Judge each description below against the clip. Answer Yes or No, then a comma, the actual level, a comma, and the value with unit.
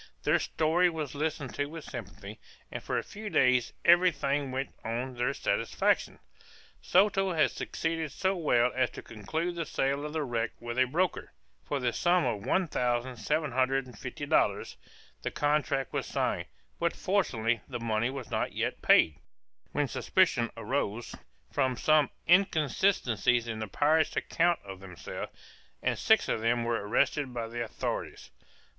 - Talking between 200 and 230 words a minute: No, average, 165 wpm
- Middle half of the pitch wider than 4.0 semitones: Yes, average, 5.2 semitones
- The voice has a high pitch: No, low, 135 Hz